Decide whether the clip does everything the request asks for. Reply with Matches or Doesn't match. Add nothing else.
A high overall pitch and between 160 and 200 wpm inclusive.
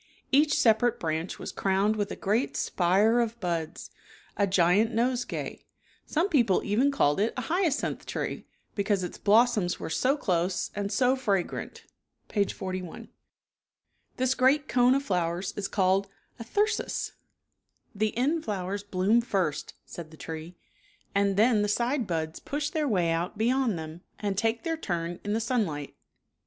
Matches